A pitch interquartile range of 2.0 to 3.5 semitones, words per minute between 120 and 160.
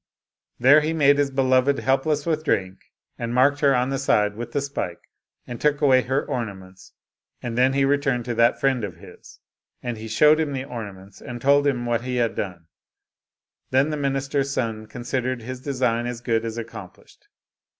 No: average, 3.2 semitones; average, 190 wpm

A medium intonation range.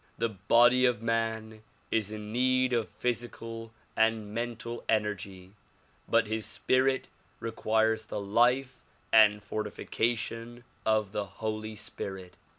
No: narrow, 1.8 semitones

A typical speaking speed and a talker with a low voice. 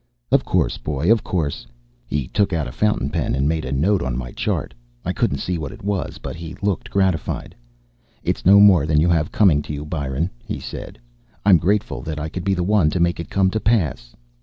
No: fast, 225 wpm; very low, 80 Hz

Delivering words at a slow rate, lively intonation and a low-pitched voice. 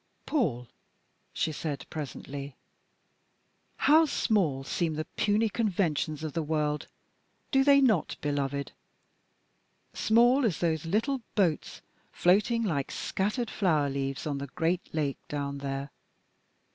No: slow, 120 wpm; wide, 7.1 semitones; medium, 160 Hz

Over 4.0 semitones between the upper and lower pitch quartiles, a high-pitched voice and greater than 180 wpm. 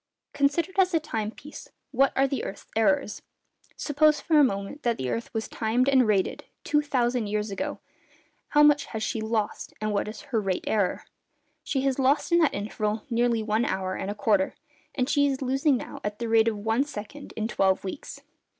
Yes: average, 4.9 semitones; high, 235 Hz; average, 200 wpm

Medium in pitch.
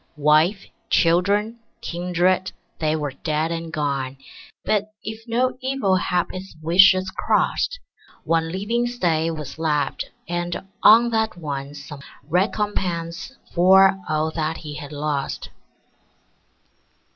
Yes: medium, 175 Hz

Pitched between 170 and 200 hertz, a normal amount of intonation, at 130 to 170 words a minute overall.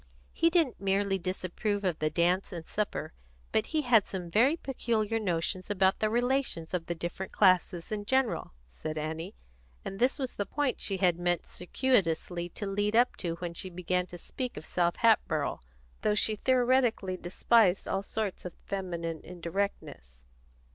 Yes: high, 190 Hz; average, 4.4 semitones; average, 165 wpm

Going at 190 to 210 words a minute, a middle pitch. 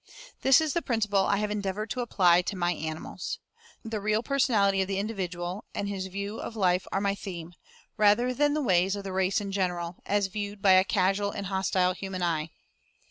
No: average, 200 wpm; high, 195 Hz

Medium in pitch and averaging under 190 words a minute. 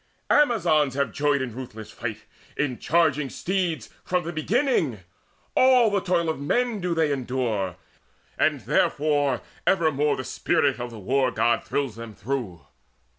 Yes: medium, 145 Hz; average, 145 wpm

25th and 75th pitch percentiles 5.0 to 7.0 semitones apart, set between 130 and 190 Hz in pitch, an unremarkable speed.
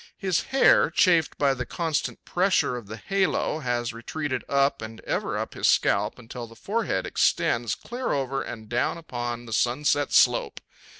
Yes: wide, 5.4 semitones; low, 135 Hz; average, 165 wpm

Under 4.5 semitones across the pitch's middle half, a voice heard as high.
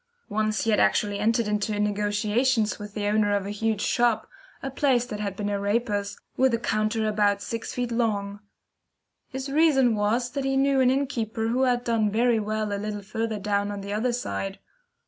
Yes: average, 2.7 semitones; high, 215 Hz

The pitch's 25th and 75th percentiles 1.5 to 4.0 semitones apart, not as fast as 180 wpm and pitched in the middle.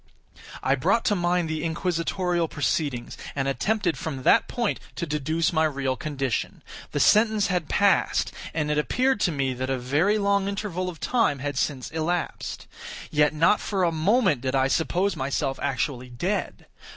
No: wide, 5.5 semitones; average, 165 wpm; medium, 160 Hz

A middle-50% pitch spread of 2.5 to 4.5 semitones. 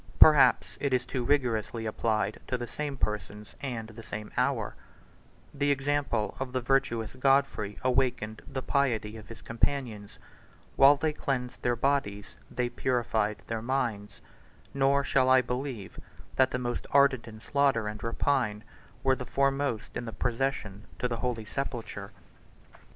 Yes: average, 3.8 semitones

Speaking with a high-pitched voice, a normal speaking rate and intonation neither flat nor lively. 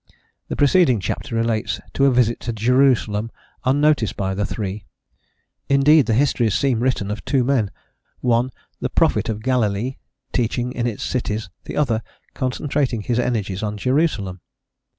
No: low, 120 Hz; average, 150 wpm; average, 3.5 semitones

